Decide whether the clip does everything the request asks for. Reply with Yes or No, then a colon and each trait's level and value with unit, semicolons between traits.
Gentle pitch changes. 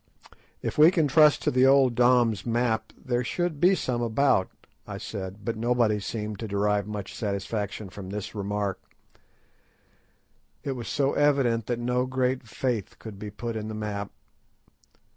No: average, 3.6 semitones